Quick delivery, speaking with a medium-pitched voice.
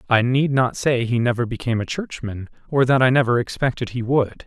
No: fast, 215 wpm; low, 125 Hz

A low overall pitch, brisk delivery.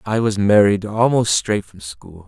No: low, 100 Hz; average, 185 wpm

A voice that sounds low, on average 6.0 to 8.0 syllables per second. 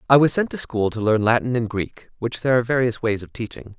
Yes: low, 120 Hz; 6.3 syllables/s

